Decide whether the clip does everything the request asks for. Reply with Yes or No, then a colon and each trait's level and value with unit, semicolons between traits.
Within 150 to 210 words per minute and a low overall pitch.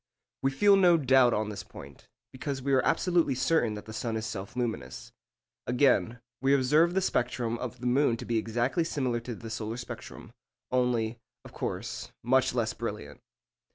Yes: average, 175 wpm; low, 125 Hz